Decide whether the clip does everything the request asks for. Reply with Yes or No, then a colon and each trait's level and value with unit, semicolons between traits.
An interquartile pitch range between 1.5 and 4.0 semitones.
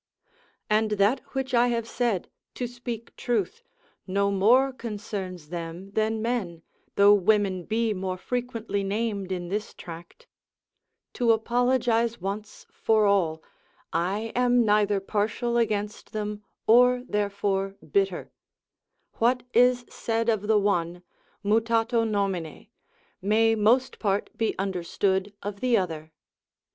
Yes: average, 3.1 semitones